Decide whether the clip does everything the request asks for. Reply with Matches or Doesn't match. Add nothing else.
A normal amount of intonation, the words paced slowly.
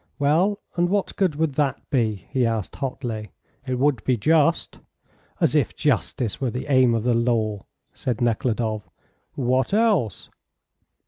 Doesn't match